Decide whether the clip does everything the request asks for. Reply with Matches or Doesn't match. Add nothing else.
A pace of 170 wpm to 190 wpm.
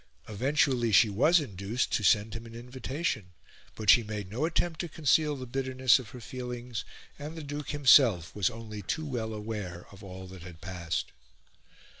Matches